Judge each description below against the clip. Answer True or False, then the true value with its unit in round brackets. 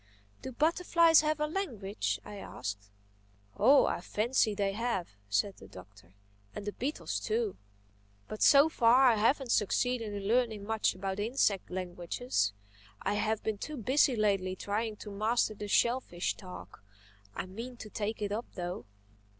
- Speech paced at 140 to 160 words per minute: True (150 wpm)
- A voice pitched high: True (215 Hz)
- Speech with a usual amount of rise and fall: True (4.7 semitones)